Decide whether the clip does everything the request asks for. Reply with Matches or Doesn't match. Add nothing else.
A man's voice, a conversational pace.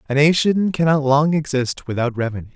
Matches